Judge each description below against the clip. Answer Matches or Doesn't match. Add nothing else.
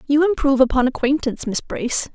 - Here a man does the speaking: Doesn't match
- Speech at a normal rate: Matches